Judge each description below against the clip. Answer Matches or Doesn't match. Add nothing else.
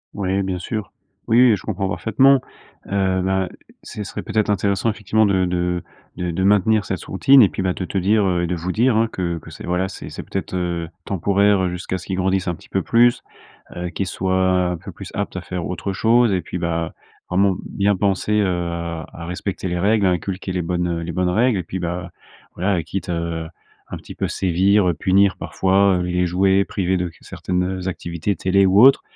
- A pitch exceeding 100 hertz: Doesn't match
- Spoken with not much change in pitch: Matches